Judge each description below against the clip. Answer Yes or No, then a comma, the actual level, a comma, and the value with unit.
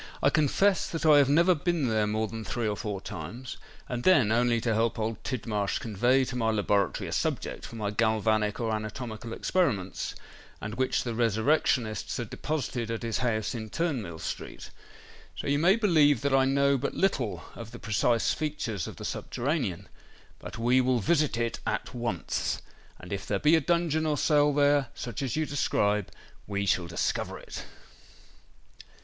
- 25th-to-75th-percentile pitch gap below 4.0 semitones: No, average, 4.8 semitones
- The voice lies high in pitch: No, low, 120 Hz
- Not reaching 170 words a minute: No, average, 175 wpm